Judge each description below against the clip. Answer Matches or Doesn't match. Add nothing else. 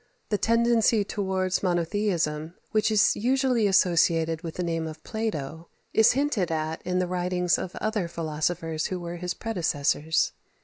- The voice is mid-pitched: Matches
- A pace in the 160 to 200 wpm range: Doesn't match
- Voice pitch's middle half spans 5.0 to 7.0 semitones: Doesn't match